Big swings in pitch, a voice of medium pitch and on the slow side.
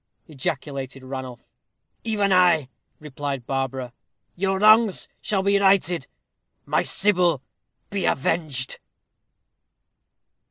Yes: wide, 6.4 semitones; medium, 160 Hz; slow, 85 wpm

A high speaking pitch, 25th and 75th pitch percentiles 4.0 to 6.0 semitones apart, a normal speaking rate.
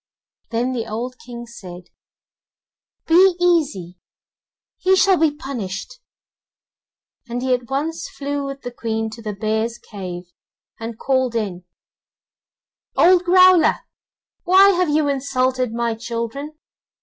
No: very high, 250 Hz; average, 5.3 semitones; slow, 120 wpm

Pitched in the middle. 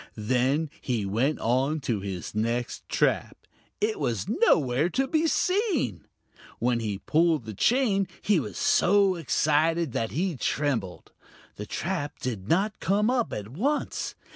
Yes: medium, 150 Hz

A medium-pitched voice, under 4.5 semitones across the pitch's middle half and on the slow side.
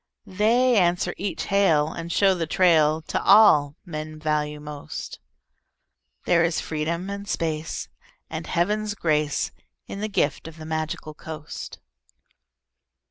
Yes: medium, 165 Hz; average, 4.1 semitones; slow, 130 wpm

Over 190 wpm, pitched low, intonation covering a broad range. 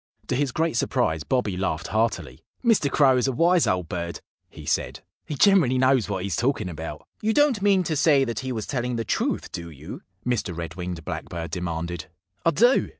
Yes: average, 200 wpm; low, 120 Hz; wide, 8.9 semitones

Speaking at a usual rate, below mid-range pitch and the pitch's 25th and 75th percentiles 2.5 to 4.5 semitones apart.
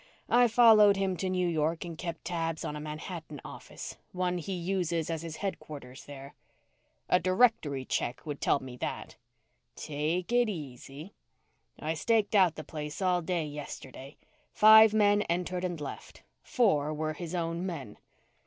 No: average, 155 wpm; medium, 170 Hz; average, 3.8 semitones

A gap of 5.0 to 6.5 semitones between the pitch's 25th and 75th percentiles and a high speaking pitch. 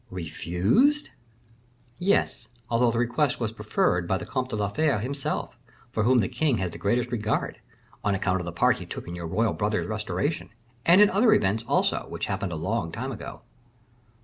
No: wide, 5.4 semitones; low, 110 Hz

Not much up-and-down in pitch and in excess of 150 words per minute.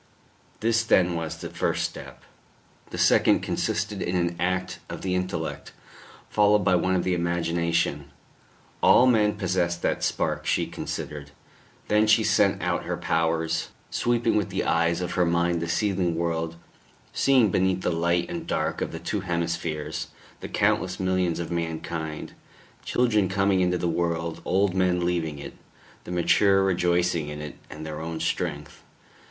Yes: narrow, 2.2 semitones; average, 160 wpm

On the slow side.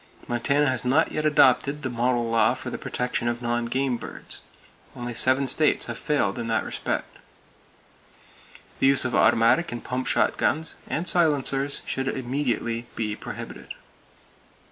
No: average, 145 wpm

